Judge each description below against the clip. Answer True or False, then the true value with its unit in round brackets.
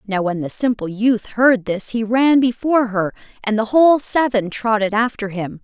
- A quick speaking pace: False (190 wpm)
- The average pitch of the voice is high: True (225 Hz)